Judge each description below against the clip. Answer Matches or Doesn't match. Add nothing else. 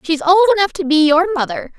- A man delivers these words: Doesn't match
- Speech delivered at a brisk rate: Matches